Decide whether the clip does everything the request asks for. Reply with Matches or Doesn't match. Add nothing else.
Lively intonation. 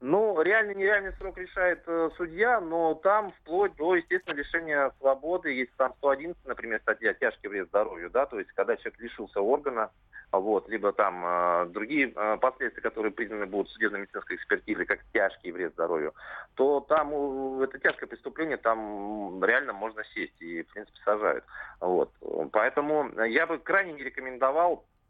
Matches